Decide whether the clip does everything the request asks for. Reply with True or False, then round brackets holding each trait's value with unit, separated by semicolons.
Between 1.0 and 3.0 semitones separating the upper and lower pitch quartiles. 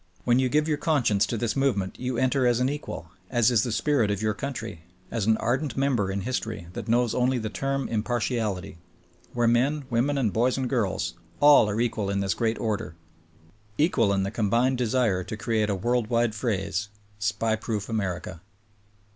False (3.7 semitones)